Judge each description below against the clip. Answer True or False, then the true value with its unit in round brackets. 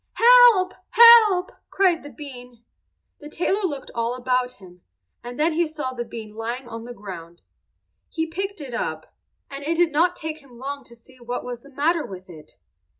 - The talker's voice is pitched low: False (275 Hz)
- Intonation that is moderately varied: False (6.0 semitones)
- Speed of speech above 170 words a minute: True (185 wpm)